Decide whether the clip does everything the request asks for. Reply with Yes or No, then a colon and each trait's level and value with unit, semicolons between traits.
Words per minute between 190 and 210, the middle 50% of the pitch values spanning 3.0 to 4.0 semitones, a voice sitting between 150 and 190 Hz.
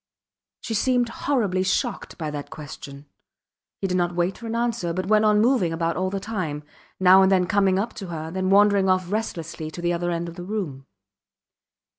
Yes: average, 200 wpm; average, 3.4 semitones; medium, 185 Hz